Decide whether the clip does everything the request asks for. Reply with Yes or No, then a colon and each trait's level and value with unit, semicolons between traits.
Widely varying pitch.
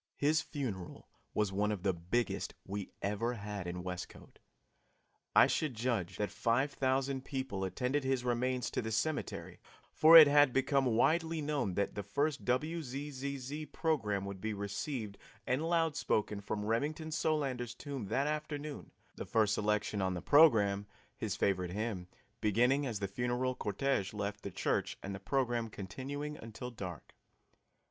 Yes: wide, 5.8 semitones